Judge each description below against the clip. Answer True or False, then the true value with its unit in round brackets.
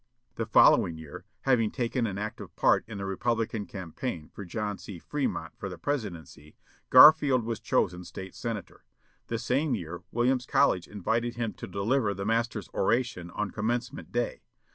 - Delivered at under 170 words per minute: True (160 wpm)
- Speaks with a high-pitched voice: False (110 Hz)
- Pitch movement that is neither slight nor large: True (3.9 semitones)